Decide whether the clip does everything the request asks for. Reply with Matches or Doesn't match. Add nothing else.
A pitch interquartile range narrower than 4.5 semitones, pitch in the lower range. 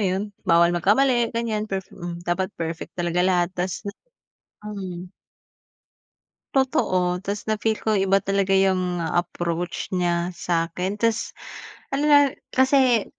Doesn't match